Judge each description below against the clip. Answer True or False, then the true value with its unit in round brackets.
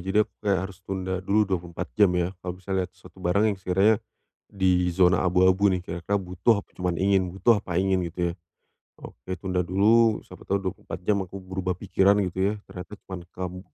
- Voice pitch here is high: False (95 Hz)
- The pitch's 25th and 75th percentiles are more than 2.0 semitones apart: False (1.5 semitones)